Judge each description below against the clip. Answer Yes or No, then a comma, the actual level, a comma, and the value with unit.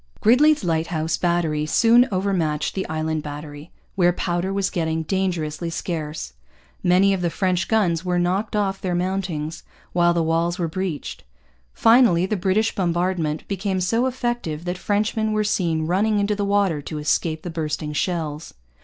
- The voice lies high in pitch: No, medium, 175 Hz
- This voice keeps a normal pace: Yes, average, 160 wpm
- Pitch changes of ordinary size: Yes, average, 3.6 semitones